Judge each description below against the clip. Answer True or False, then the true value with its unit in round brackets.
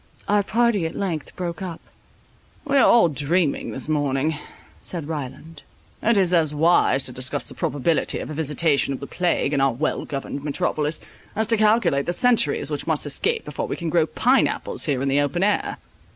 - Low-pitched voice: False (160 Hz)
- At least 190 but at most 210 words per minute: True (195 wpm)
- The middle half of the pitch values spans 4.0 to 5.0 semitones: True (4.6 semitones)